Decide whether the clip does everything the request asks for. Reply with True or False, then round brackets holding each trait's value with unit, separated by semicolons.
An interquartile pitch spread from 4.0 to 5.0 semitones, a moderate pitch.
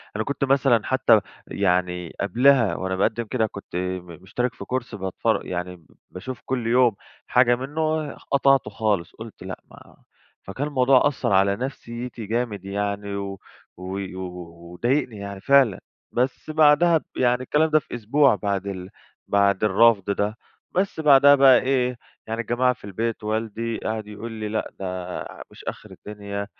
False (4.5 semitones; 110 Hz)